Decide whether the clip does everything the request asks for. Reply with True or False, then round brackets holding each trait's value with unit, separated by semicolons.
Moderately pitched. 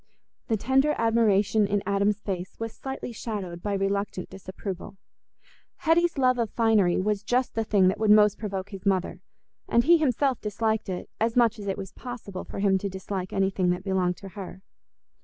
False (205 Hz)